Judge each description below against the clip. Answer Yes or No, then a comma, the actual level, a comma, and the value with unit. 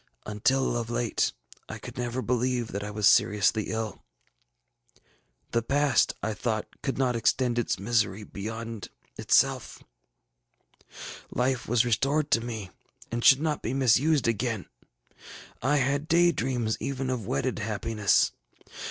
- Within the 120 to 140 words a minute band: Yes, slow, 135 wpm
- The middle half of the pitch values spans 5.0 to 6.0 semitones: No, average, 3.2 semitones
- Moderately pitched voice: No, low, 120 Hz